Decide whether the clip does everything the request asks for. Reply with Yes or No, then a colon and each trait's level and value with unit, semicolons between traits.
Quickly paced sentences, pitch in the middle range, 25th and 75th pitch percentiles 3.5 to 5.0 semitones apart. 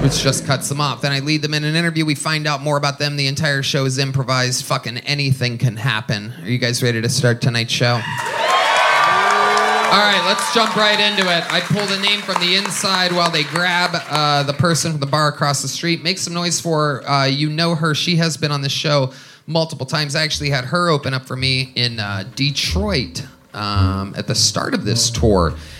Yes: fast, 225 wpm; medium, 145 Hz; average, 4.1 semitones